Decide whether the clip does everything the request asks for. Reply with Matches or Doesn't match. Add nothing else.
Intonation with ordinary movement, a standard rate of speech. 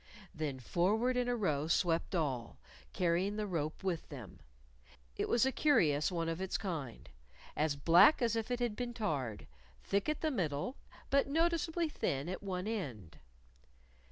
Doesn't match